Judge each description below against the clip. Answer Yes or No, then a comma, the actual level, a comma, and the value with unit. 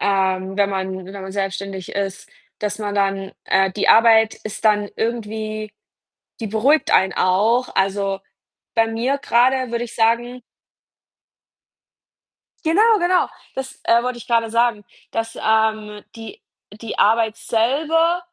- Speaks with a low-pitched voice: No, high, 220 Hz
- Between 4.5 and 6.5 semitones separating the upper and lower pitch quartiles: No, average, 3.0 semitones